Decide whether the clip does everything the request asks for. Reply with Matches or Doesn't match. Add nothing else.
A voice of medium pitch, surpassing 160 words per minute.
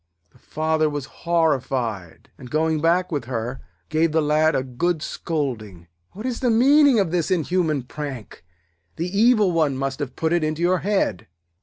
Matches